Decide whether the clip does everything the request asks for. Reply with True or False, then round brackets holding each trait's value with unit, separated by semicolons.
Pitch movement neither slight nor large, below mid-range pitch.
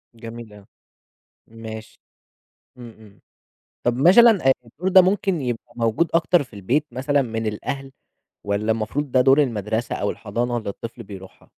True (4.3 semitones; 120 Hz)